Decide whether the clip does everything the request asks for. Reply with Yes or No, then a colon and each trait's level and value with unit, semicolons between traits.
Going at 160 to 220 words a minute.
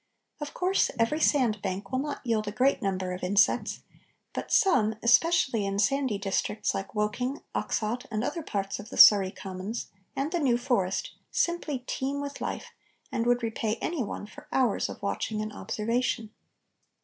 Yes: average, 170 wpm